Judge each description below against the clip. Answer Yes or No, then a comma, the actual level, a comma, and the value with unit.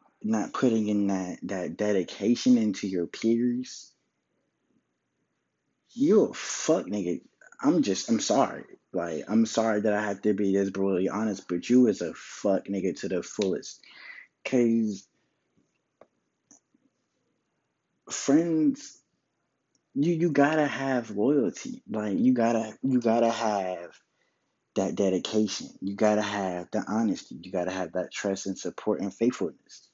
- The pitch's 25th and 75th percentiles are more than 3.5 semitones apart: Yes, average, 4.1 semitones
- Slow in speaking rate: Yes, slow, 130 wpm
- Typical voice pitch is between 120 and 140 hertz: No, low, 110 Hz